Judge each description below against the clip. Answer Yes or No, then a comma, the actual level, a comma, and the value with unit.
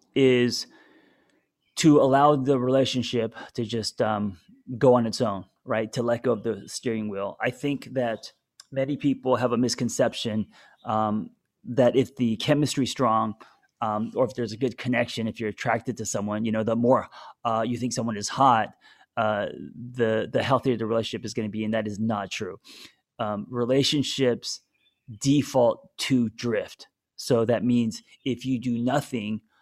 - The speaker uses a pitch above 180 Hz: No, low, 120 Hz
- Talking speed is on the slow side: No, average, 170 wpm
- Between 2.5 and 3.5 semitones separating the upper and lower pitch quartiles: Yes, average, 2.8 semitones